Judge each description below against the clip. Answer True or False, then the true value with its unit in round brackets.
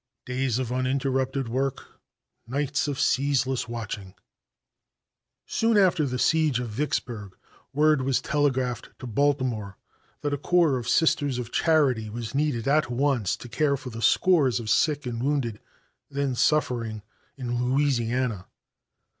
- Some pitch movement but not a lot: True (3.3 semitones)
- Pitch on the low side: True (130 Hz)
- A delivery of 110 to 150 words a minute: True (135 wpm)